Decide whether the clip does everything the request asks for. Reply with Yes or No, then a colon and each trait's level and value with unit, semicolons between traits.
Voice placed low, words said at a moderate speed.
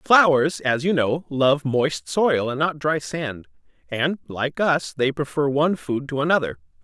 No: medium, 145 Hz; average, 175 wpm